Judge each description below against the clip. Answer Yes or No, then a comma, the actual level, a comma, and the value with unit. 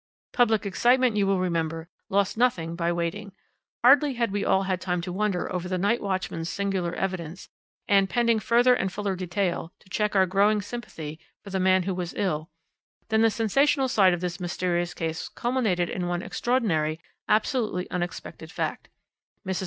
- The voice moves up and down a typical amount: Yes, average, 3.5 semitones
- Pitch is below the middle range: No, high, 190 Hz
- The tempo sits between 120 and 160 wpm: No, average, 170 wpm